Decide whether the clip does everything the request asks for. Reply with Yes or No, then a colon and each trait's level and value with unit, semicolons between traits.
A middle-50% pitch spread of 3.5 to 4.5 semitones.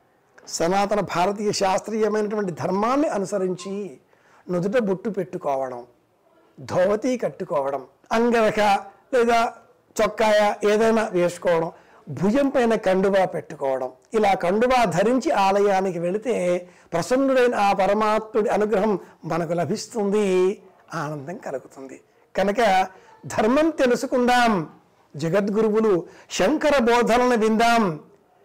Yes: average, 3.9 semitones